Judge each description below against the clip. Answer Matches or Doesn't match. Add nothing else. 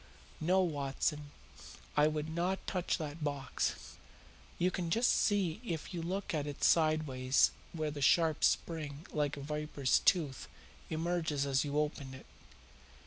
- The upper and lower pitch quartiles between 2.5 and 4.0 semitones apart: Matches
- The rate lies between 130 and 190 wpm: Matches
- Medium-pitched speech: Matches